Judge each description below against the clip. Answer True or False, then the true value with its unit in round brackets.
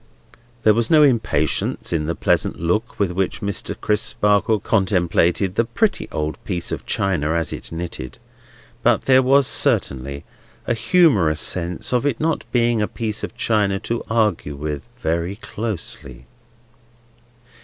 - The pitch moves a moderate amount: False (5.8 semitones)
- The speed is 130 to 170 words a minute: True (145 wpm)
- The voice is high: False (100 Hz)